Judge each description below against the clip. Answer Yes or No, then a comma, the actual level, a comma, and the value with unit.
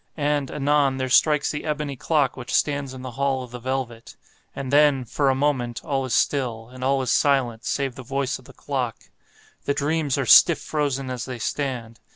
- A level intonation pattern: Yes, narrow, 2.1 semitones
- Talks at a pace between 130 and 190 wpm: No, average, 200 wpm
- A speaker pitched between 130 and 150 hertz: Yes, low, 135 Hz